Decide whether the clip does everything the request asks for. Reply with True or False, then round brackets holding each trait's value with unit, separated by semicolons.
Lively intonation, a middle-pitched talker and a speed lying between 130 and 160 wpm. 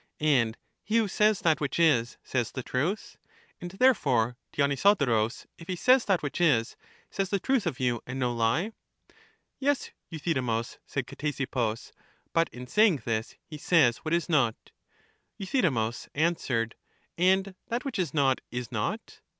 True (7.3 semitones; 150 Hz; 150 wpm)